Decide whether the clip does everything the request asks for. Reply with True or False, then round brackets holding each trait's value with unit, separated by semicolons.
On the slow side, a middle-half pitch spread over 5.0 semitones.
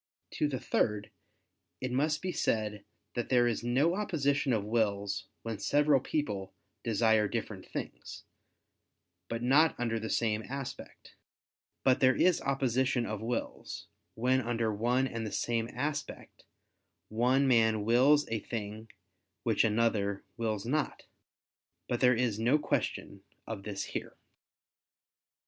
False (130 wpm; 3.4 semitones)